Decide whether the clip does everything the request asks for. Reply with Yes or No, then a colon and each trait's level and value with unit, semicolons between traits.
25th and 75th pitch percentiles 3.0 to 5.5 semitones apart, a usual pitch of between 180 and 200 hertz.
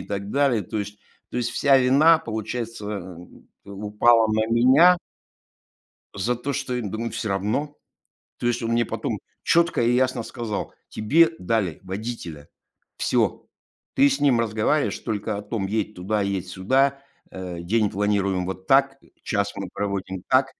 No: average, 4.2 semitones; low, 110 Hz